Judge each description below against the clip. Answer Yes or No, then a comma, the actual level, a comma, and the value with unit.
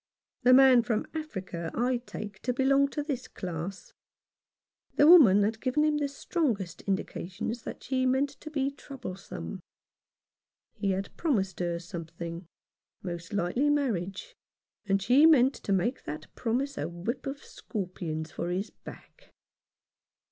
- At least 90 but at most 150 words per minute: Yes, average, 140 wpm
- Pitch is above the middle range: Yes, high, 225 Hz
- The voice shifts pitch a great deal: Yes, wide, 6.9 semitones